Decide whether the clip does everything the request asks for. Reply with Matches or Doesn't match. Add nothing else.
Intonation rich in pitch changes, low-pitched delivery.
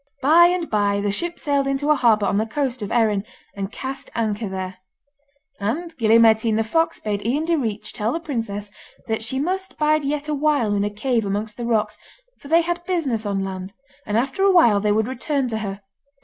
Doesn't match